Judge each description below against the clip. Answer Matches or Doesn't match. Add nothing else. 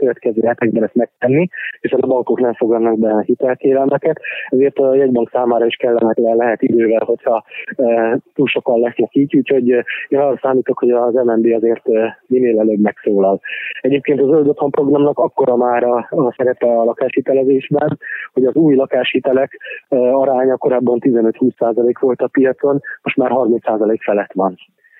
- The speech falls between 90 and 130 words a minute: Doesn't match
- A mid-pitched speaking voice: Doesn't match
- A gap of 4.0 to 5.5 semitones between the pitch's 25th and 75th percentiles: Doesn't match